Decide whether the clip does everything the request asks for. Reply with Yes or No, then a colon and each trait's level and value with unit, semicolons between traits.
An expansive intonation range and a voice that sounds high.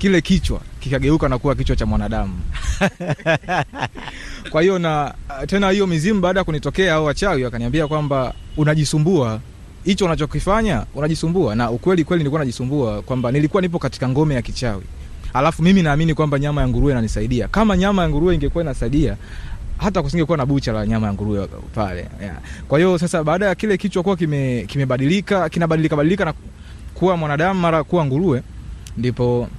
No: wide, 6.5 semitones; medium, 145 Hz